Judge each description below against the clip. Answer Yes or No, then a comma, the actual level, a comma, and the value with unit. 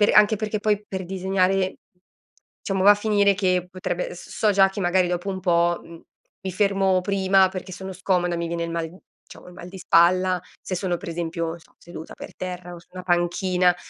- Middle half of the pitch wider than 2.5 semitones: No, narrow, 1.7 semitones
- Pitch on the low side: No, medium, 185 Hz